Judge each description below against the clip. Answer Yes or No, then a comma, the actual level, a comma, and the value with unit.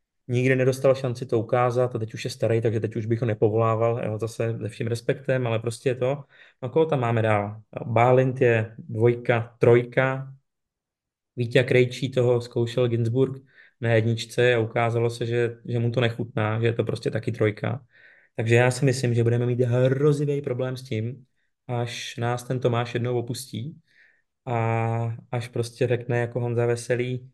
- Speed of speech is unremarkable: No, fast, 175 wpm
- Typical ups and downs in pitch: No, narrow, 1.8 semitones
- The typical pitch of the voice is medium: No, low, 120 Hz